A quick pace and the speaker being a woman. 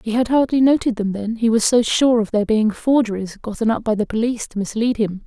Yes: fast, 250 wpm; female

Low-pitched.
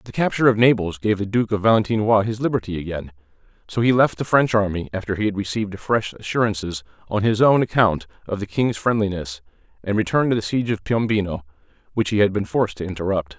Yes: low, 105 Hz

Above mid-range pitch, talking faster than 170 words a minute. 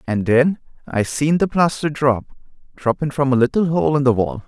No: low, 135 Hz; average, 200 wpm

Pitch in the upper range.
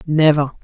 No: medium, 150 Hz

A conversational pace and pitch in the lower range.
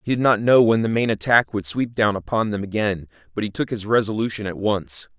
No: fast, 245 wpm; low, 105 Hz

